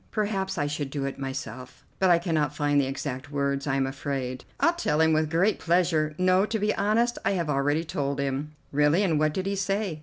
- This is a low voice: No, medium, 155 Hz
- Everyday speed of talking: No, fast, 220 wpm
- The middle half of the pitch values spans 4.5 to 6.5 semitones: Yes, average, 5.0 semitones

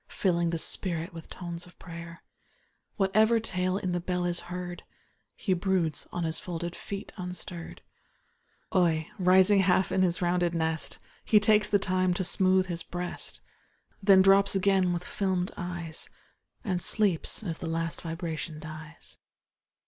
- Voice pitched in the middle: Yes, medium, 180 Hz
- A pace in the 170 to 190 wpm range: No, average, 150 wpm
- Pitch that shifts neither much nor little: No, narrow, 2.0 semitones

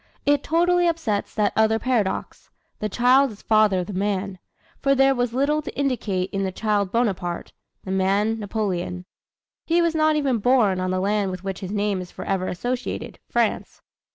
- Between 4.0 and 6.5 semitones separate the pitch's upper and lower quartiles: Yes, wide, 5.4 semitones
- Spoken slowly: No, average, 180 wpm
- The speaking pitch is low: No, high, 215 Hz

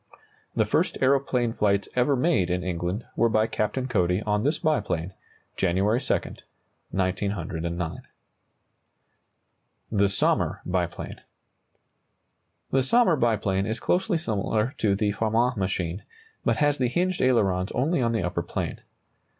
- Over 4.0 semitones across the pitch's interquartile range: Yes, wide, 5.6 semitones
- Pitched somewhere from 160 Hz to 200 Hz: No, low, 105 Hz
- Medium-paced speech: No, slow, 125 wpm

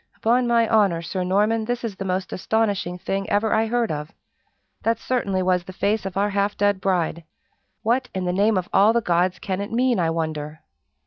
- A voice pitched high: Yes, high, 200 Hz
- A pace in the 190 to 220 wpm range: Yes, fast, 205 wpm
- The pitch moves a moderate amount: Yes, average, 3.6 semitones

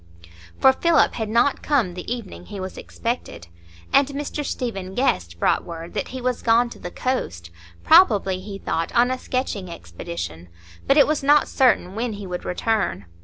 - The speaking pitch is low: No, high, 215 Hz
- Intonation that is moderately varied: No, wide, 6.6 semitones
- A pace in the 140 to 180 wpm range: Yes, average, 170 wpm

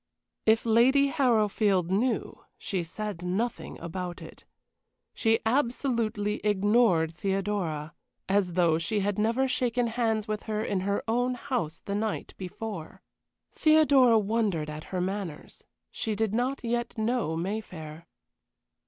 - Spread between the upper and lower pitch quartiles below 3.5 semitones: No, average, 4.2 semitones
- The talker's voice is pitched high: Yes, high, 210 Hz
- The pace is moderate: No, slow, 125 wpm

